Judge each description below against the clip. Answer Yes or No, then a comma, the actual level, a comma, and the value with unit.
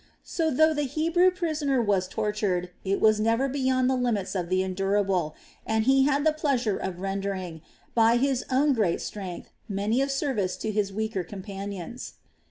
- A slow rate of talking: No, average, 170 wpm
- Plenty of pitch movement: Yes, wide, 5.7 semitones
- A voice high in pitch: Yes, high, 220 Hz